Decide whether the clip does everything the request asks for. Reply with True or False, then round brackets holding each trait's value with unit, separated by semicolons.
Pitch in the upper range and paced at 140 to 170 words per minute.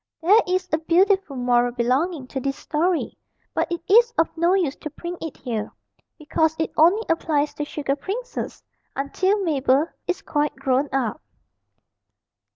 True (315 Hz; 155 wpm)